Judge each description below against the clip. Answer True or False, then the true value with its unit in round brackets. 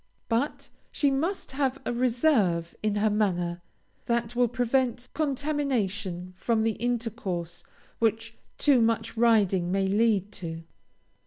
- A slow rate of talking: True (125 wpm)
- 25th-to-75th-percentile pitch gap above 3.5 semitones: True (4.2 semitones)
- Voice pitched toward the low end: False (225 Hz)